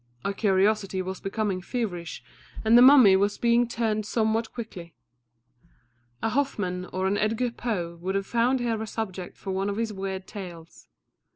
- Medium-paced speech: Yes, average, 165 wpm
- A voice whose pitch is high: Yes, high, 205 Hz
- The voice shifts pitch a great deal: No, average, 3.4 semitones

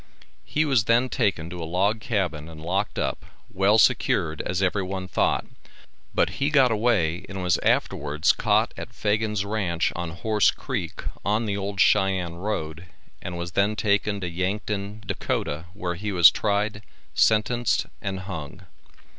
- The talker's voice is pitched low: Yes, low, 100 Hz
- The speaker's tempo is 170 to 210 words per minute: No, average, 155 wpm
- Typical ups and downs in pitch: Yes, average, 3.4 semitones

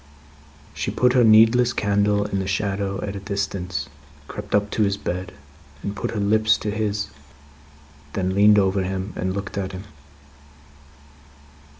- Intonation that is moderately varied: No, narrow, 1.5 semitones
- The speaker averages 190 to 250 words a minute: No, average, 155 wpm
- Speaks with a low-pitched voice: Yes, low, 100 Hz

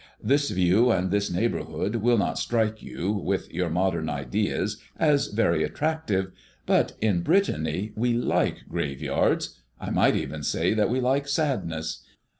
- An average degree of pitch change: No, wide, 5.7 semitones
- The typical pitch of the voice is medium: No, low, 105 Hz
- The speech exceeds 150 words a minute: No, average, 145 wpm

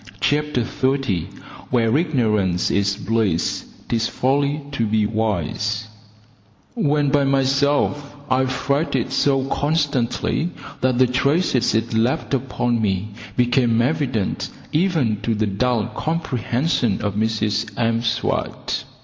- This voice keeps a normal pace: No, slow, 110 wpm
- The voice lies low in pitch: Yes, low, 125 Hz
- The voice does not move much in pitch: No, average, 4.2 semitones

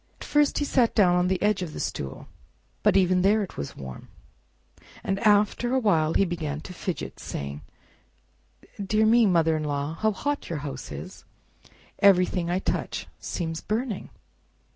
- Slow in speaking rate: No, average, 165 wpm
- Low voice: No, medium, 185 Hz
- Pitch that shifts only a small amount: No, average, 5.0 semitones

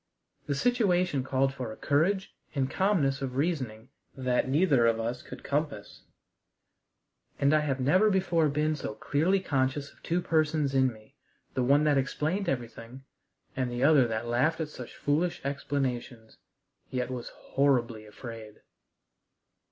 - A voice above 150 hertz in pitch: No, medium, 140 Hz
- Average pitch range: Yes, average, 3.8 semitones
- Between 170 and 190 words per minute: No, average, 145 wpm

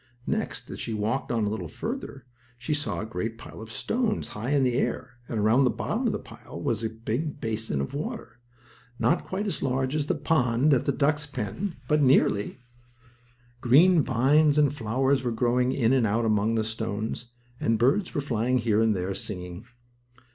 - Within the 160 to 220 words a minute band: Yes, average, 190 wpm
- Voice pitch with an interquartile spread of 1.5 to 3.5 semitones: No, average, 4.4 semitones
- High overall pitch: No, low, 120 Hz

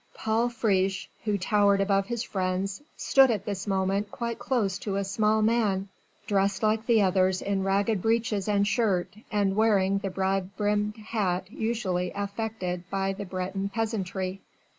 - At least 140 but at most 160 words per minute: Yes, average, 155 wpm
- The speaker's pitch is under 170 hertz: No, high, 200 Hz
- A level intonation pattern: Yes, narrow, 2.3 semitones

